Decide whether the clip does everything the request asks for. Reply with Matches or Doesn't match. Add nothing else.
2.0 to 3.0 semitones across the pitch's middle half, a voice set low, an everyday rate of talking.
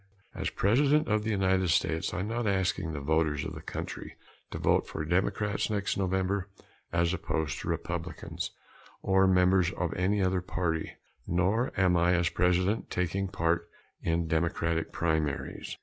Matches